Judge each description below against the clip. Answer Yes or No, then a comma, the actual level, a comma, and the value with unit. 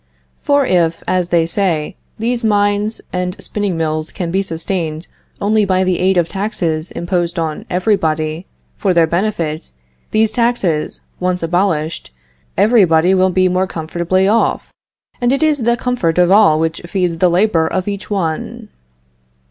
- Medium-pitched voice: Yes, medium, 180 Hz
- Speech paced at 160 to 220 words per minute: No, average, 150 wpm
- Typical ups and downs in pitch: Yes, average, 3.7 semitones